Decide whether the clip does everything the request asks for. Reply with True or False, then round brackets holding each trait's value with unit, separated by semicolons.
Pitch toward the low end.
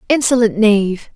False (225 Hz)